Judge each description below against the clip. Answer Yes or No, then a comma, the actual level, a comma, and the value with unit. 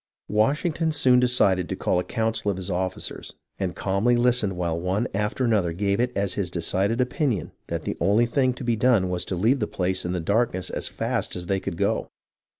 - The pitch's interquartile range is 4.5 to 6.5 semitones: Yes, average, 4.8 semitones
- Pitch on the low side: Yes, low, 100 Hz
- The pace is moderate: No, fast, 210 wpm